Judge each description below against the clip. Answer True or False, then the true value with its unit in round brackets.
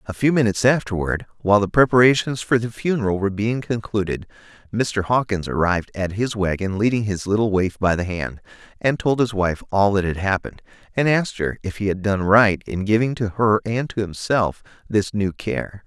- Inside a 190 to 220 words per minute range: True (195 wpm)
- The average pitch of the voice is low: True (105 Hz)